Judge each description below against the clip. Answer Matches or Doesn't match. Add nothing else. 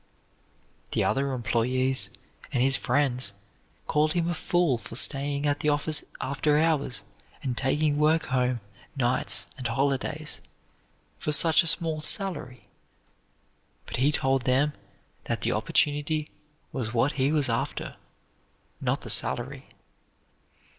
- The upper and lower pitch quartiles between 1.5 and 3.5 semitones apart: Matches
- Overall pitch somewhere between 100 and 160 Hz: Matches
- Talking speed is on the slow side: Matches